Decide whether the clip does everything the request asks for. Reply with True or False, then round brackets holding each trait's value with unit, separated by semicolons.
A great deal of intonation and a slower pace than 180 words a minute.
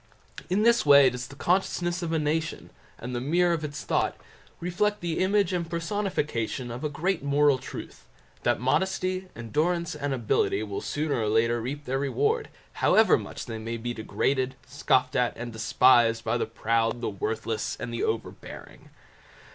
True (6.5 semitones; 165 wpm)